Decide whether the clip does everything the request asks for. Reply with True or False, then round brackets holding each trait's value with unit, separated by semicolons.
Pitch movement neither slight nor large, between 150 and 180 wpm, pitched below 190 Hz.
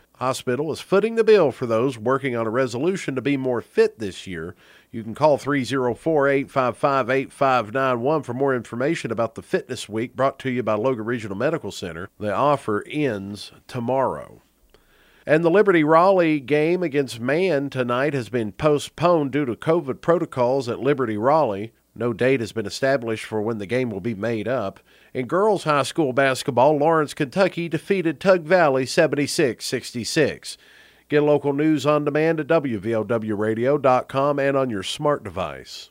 True (4.5 semitones; 160 wpm; 135 Hz)